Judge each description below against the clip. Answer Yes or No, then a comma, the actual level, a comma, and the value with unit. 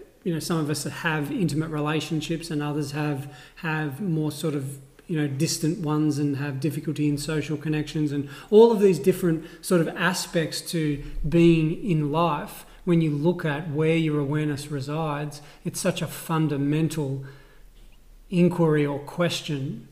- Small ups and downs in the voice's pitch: Yes, narrow, 2.3 semitones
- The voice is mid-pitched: Yes, medium, 155 Hz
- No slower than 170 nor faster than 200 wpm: No, average, 155 wpm